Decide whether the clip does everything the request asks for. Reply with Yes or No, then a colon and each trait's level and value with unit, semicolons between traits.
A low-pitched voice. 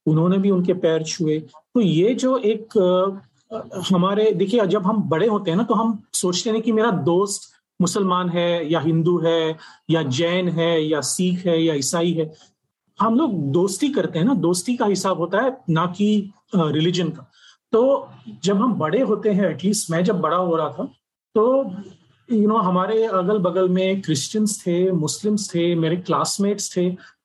No: medium, 185 Hz